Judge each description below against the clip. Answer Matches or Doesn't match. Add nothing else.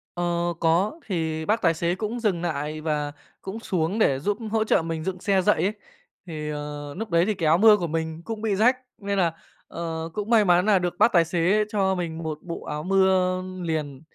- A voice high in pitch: Doesn't match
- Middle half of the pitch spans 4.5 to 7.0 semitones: Doesn't match